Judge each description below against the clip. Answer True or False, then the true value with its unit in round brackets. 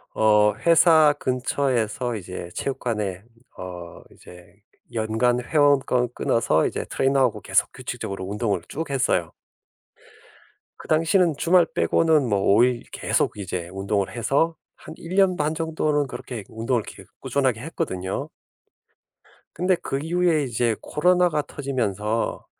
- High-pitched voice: False (125 Hz)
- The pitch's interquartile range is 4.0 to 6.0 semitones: False (6.6 semitones)